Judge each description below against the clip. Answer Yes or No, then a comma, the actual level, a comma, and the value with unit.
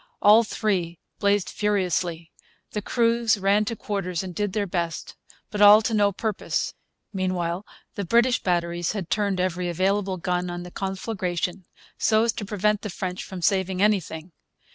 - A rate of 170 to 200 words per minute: No, average, 160 wpm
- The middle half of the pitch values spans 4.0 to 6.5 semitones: No, average, 2.8 semitones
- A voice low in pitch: No, high, 195 Hz